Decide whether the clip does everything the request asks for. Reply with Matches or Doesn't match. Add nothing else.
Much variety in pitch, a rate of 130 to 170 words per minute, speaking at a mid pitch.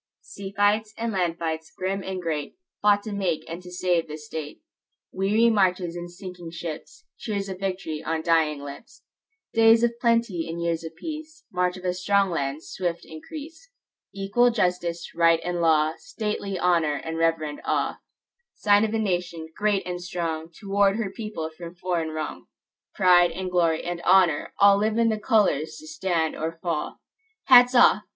Doesn't match